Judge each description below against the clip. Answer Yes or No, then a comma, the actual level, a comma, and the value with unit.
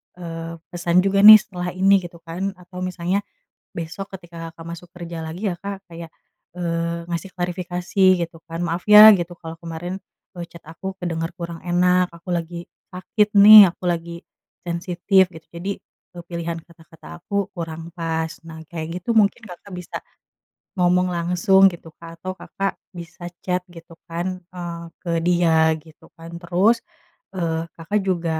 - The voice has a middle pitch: Yes, medium, 175 Hz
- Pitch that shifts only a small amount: Yes, narrow, 1.5 semitones